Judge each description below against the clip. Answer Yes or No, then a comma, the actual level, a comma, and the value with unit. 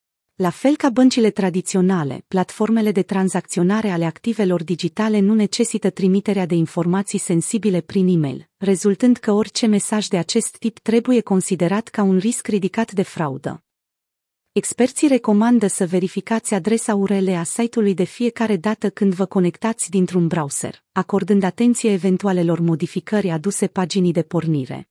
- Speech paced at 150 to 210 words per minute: No, average, 140 wpm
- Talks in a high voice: Yes, high, 195 Hz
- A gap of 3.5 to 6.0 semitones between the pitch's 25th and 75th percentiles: No, average, 3.1 semitones